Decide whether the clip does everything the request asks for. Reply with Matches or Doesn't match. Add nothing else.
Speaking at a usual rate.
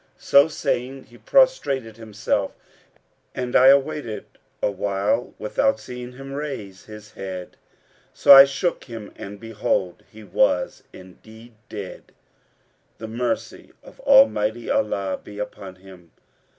Doesn't match